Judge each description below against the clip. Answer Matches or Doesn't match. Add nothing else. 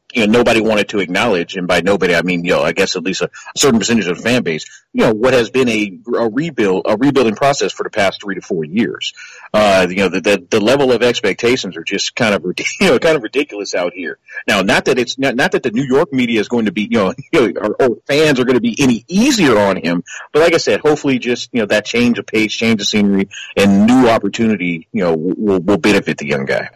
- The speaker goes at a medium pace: Doesn't match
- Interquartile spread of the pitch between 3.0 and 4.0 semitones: Matches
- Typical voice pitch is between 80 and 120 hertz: Matches